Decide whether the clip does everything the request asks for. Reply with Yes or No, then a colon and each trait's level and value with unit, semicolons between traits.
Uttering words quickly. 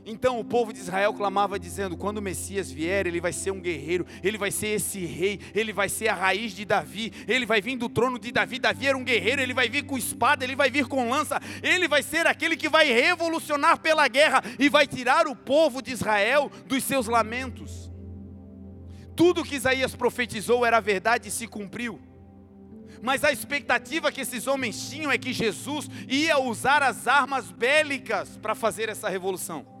Yes: fast, 195 wpm